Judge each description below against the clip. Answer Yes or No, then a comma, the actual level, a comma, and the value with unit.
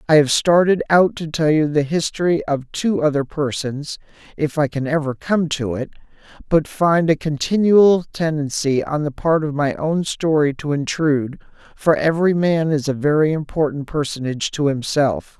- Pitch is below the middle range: No, medium, 150 Hz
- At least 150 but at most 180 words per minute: Yes, average, 165 wpm